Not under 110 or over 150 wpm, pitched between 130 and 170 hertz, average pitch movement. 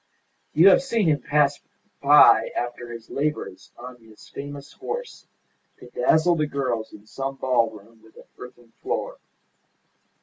Yes: average, 140 wpm; low, 135 Hz; average, 4.4 semitones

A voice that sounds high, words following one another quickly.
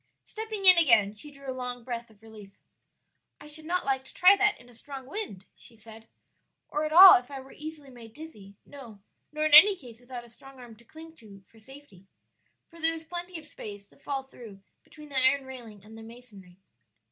Yes: very high, 260 Hz; fast, 215 wpm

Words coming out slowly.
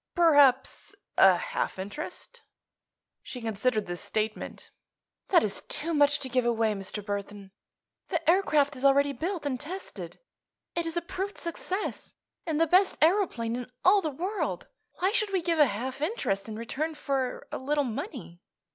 No: average, 160 wpm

